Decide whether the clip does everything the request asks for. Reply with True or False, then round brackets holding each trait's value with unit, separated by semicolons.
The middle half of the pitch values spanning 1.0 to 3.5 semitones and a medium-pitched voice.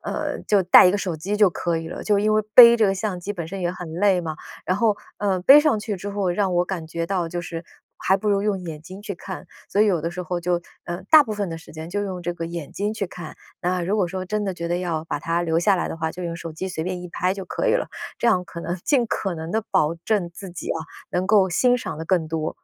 True (3.1 semitones; 180 Hz)